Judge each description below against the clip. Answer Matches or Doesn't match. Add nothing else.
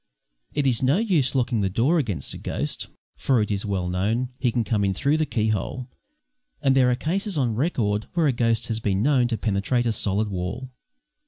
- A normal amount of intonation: Matches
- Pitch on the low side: Matches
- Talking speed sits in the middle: Doesn't match